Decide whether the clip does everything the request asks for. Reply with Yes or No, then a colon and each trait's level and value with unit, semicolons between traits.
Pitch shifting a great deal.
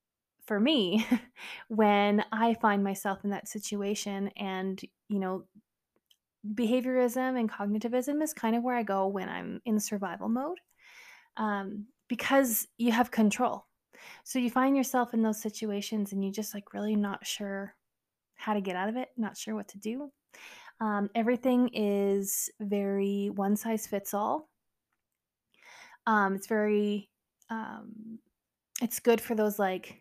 No: average, 3.2 semitones